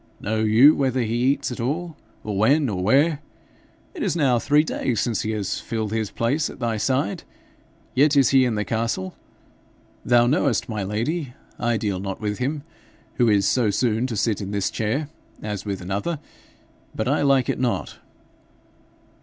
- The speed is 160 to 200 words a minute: Yes, average, 180 wpm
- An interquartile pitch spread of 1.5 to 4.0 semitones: No, average, 4.5 semitones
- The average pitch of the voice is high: No, low, 115 Hz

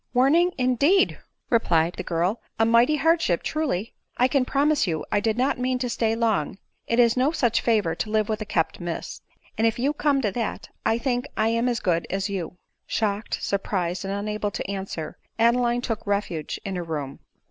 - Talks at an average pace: No, fast, 210 wpm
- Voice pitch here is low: No, high, 225 Hz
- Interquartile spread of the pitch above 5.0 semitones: No, average, 4.5 semitones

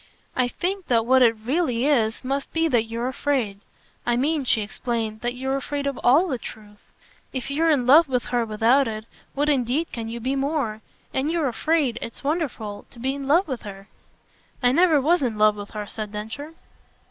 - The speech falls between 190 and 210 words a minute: Yes, average, 200 wpm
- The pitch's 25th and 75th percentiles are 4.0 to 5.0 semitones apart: Yes, average, 4.3 semitones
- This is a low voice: No, very high, 255 Hz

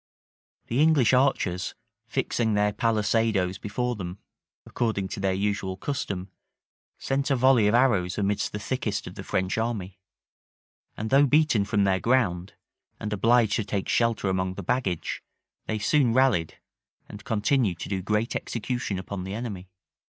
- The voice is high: No, low, 105 Hz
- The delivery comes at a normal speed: Yes, average, 150 wpm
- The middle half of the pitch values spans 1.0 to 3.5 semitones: No, average, 4.0 semitones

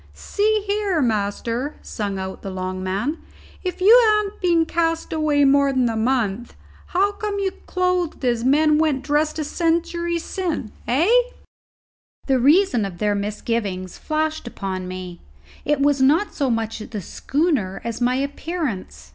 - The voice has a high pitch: Yes, very high, 280 Hz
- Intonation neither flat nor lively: No, wide, 7.6 semitones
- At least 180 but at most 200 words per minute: No, average, 150 wpm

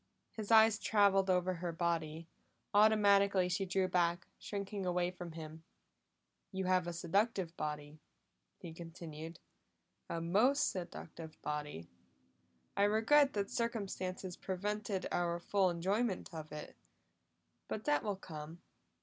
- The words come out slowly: Yes, slow, 125 wpm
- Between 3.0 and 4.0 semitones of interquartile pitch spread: Yes, average, 3.4 semitones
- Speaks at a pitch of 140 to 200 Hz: Yes, medium, 185 Hz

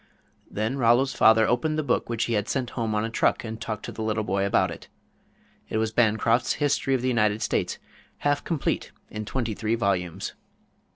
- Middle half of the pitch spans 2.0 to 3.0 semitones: Yes, narrow, 2.6 semitones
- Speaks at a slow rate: No, average, 195 wpm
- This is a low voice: Yes, low, 115 Hz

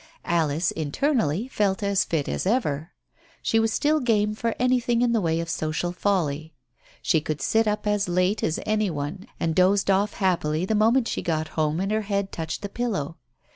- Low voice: No, high, 195 Hz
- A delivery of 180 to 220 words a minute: Yes, average, 190 wpm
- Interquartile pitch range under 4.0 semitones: No, average, 5.1 semitones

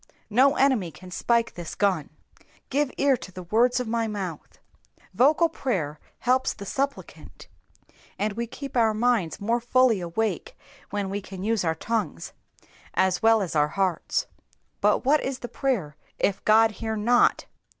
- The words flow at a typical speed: Yes, average, 160 wpm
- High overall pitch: Yes, high, 220 Hz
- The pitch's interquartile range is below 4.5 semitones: No, average, 4.9 semitones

